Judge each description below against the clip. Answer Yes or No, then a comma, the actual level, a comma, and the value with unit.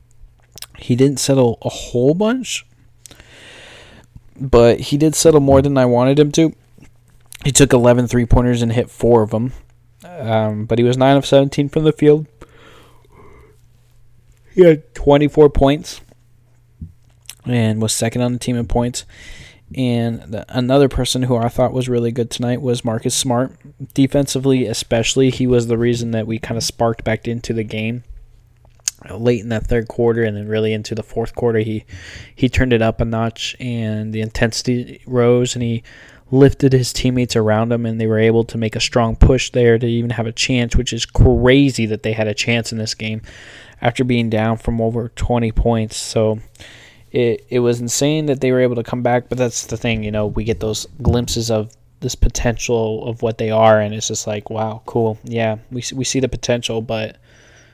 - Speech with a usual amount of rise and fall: No, narrow, 1.9 semitones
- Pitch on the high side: No, low, 120 Hz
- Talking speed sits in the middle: Yes, average, 190 wpm